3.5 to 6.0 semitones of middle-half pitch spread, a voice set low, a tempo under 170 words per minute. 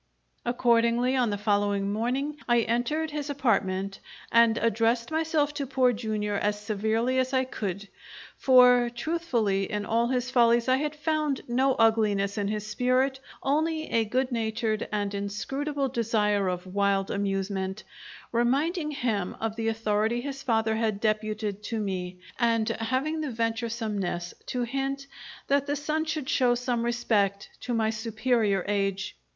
No: average, 3.9 semitones; high, 230 Hz; average, 145 wpm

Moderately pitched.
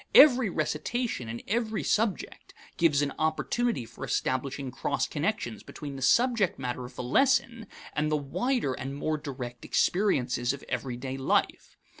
Yes: medium, 150 Hz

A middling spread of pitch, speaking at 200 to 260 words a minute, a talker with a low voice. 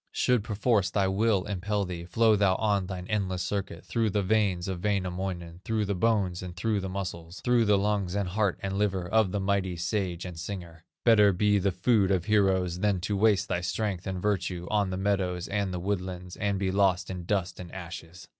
No: narrow, 2.3 semitones; fast, 205 wpm; very low, 95 Hz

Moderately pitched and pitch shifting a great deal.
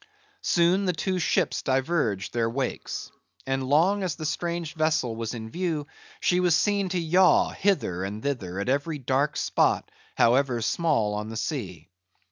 Yes: medium, 145 Hz; wide, 7.1 semitones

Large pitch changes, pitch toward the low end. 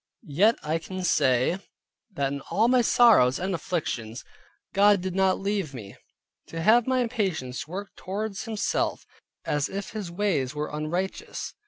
No: wide, 5.7 semitones; medium, 185 Hz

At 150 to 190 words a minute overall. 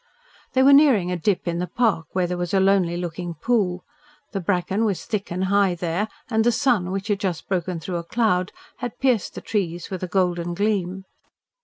No: fast, 205 wpm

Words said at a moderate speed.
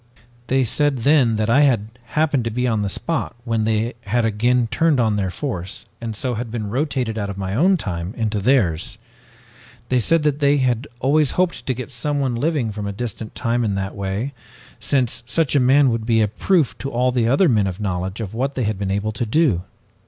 No: fast, 220 wpm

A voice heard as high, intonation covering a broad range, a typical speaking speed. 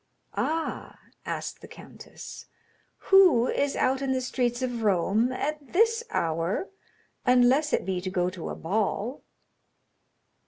No: very high, 250 Hz; wide, 6.3 semitones; slow, 130 wpm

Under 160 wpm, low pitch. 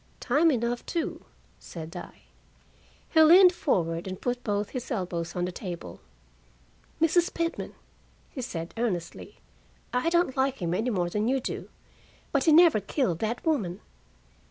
No: average, 150 wpm; high, 235 Hz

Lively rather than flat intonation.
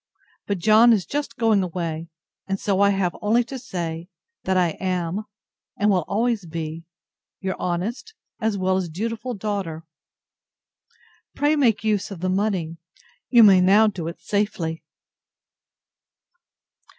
No: average, 3.8 semitones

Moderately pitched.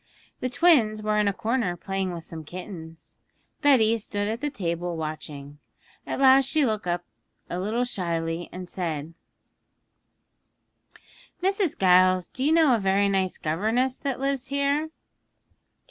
No: high, 205 Hz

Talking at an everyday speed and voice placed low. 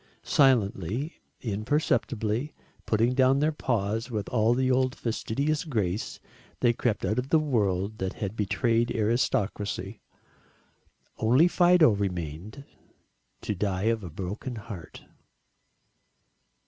No: slow, 110 wpm; low, 115 Hz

